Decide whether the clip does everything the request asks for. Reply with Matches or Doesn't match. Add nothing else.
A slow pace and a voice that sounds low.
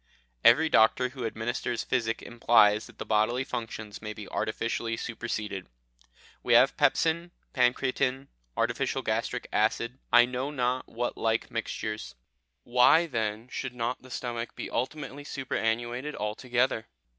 Matches